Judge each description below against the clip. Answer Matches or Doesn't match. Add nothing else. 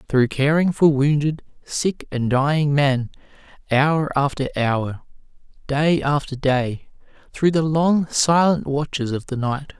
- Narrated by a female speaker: Doesn't match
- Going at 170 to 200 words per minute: Doesn't match